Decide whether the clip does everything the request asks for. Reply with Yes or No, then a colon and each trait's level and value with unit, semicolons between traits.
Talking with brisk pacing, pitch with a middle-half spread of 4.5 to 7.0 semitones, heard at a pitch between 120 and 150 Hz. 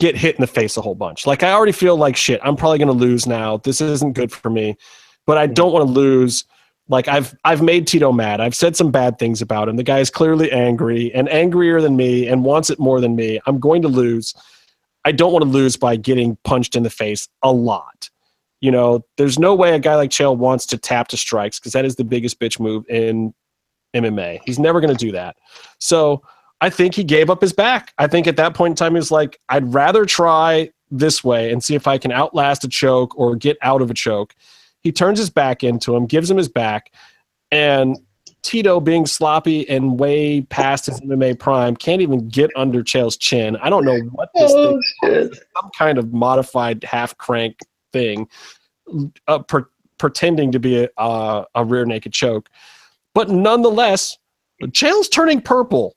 Yes: fast, 210 wpm; average, 4.8 semitones; low, 135 Hz